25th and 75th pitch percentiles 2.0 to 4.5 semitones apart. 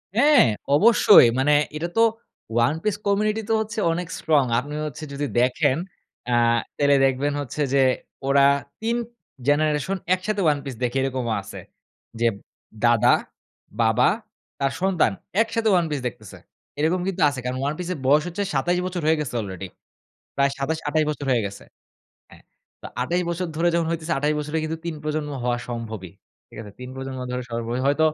No: average, 5.0 semitones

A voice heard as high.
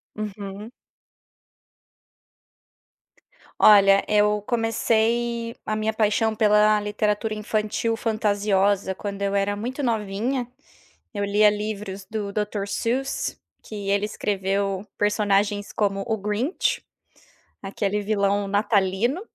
Yes: high, 210 Hz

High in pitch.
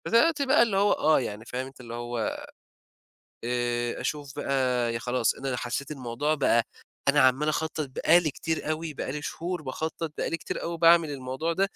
No: medium, 140 Hz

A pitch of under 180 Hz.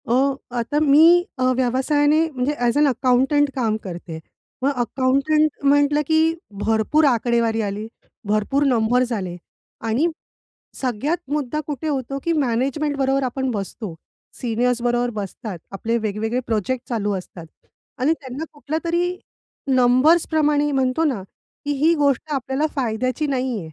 No: very high, 260 Hz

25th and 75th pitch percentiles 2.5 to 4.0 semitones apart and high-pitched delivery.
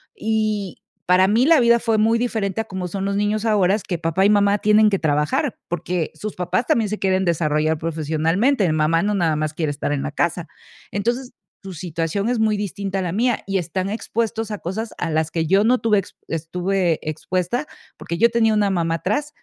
No: average, 4.6 semitones; high, 195 Hz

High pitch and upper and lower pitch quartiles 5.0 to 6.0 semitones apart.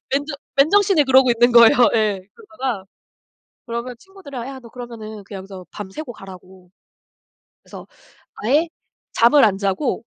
Yes: high, 240 Hz; average, 5.3 semitones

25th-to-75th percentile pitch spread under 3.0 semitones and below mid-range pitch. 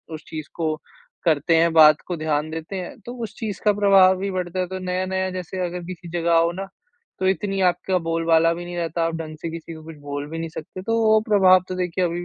No: narrow, 2.4 semitones; medium, 175 Hz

